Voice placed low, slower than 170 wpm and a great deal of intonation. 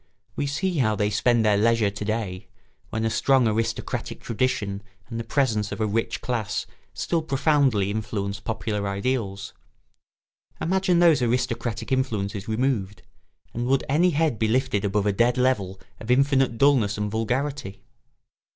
No: low, 115 Hz; average, 150 wpm; average, 4.2 semitones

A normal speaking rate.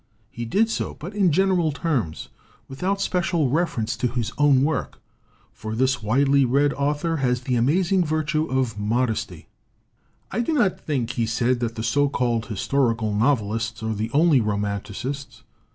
Yes: average, 165 wpm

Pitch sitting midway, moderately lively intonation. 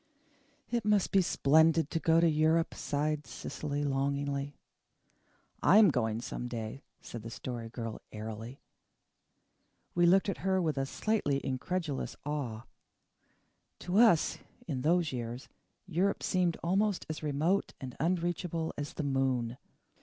Yes: medium, 150 Hz; average, 4.8 semitones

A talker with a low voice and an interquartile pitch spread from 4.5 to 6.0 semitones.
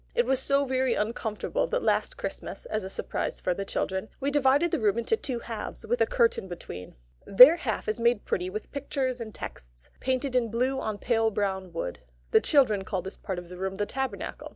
No: high, 225 Hz; wide, 5.4 semitones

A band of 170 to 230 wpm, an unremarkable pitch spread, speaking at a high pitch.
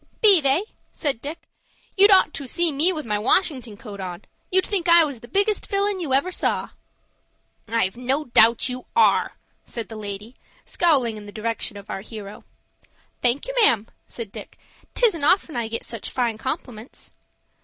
No: average, 175 wpm; wide, 7.5 semitones; very high, 255 Hz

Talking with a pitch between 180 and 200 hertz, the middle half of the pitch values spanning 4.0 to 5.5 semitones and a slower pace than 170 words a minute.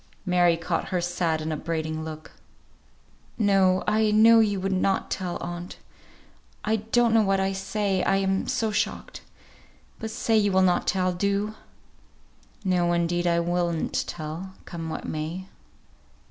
No: medium, 185 Hz; average, 2.7 semitones; average, 150 wpm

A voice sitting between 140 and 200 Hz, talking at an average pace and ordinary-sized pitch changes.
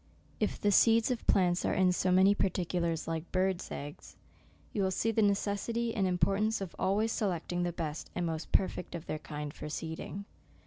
Yes: medium, 185 Hz; average, 195 wpm; average, 3.1 semitones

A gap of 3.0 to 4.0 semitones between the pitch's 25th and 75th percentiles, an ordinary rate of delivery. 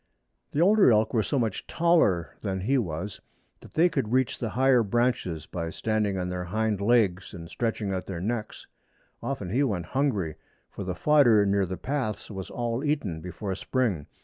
No: wide, 5.4 semitones; average, 180 wpm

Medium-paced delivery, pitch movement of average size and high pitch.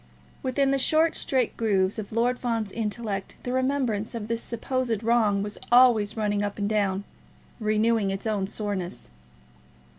Yes: average, 150 wpm; average, 3.0 semitones; high, 220 Hz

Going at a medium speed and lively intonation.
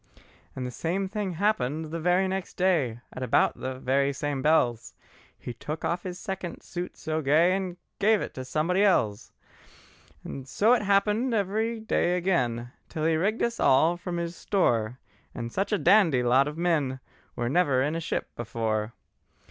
Yes: average, 170 wpm; wide, 6.6 semitones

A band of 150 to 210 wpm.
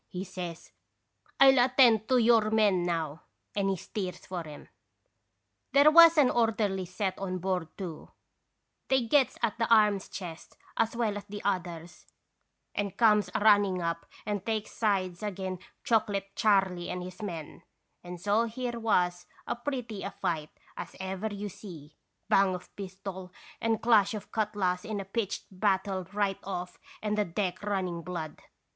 Yes: average, 160 wpm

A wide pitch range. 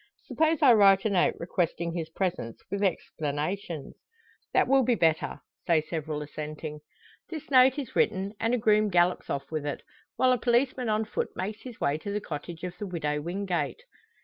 Yes: wide, 6.0 semitones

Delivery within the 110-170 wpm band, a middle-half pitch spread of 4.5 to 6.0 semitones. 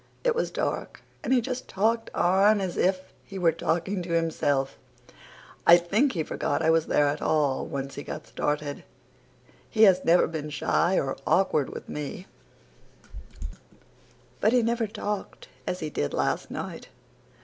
Yes: average, 160 wpm; wide, 5.4 semitones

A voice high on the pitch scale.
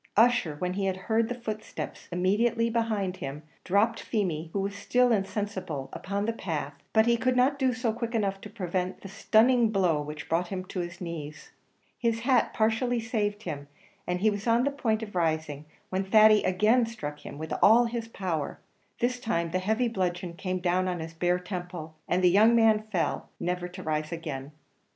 Yes: high, 195 Hz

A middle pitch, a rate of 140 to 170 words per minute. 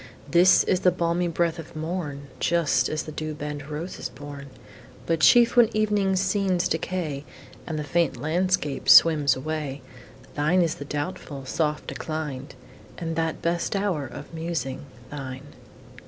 Yes: medium, 160 Hz; average, 150 wpm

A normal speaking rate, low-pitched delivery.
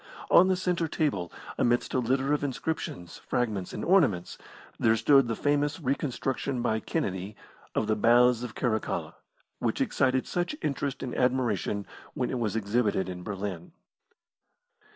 Yes: average, 145 wpm; low, 125 Hz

